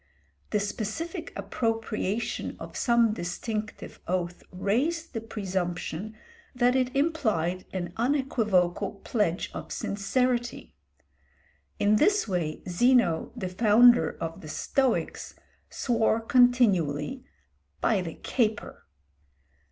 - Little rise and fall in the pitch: No, average, 5.2 semitones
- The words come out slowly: Yes, slow, 95 wpm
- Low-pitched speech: No, high, 215 Hz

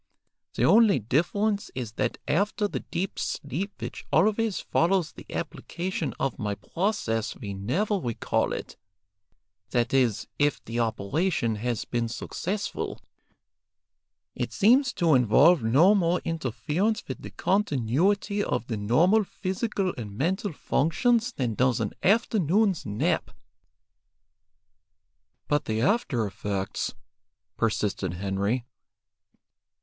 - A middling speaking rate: No, slow, 115 wpm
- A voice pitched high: No, medium, 150 Hz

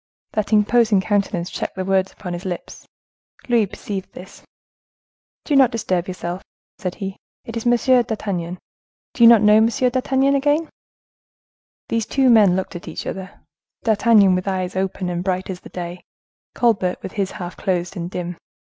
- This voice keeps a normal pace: Yes, average, 155 wpm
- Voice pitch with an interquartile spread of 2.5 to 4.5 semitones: Yes, average, 4.0 semitones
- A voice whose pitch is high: Yes, high, 195 Hz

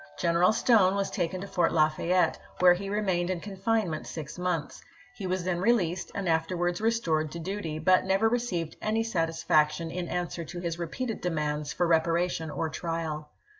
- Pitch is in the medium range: Yes, medium, 175 Hz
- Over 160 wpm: Yes, average, 170 wpm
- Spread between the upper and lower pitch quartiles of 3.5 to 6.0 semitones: No, average, 2.9 semitones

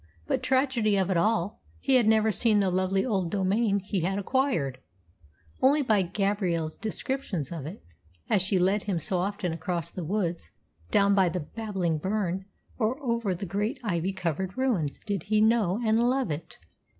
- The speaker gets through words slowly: No, average, 175 wpm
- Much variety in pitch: No, average, 3.6 semitones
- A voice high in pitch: Yes, high, 195 Hz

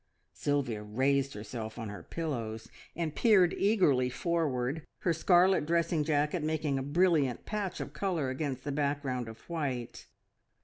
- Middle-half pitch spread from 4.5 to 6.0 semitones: Yes, average, 4.8 semitones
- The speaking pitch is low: No, medium, 145 Hz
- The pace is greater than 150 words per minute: No, average, 140 wpm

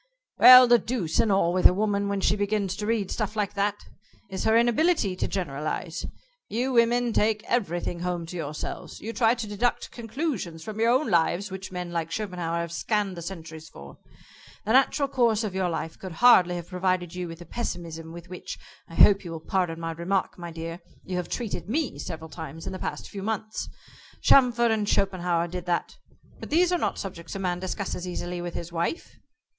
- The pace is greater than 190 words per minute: Yes, average, 200 wpm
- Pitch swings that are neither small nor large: Yes, average, 4.3 semitones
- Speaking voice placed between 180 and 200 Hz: Yes, high, 190 Hz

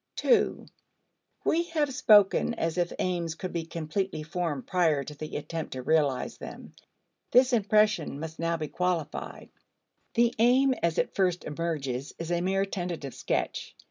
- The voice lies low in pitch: No, medium, 170 Hz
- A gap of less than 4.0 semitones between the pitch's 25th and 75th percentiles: No, average, 4.3 semitones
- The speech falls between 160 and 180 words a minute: No, average, 150 wpm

